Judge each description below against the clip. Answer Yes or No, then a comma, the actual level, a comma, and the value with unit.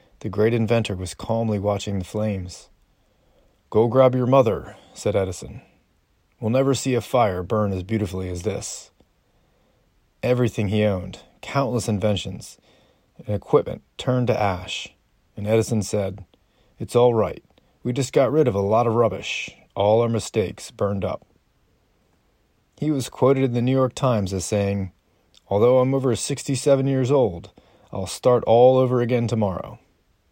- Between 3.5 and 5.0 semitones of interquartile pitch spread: Yes, average, 3.9 semitones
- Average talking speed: Yes, average, 150 wpm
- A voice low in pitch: Yes, low, 110 Hz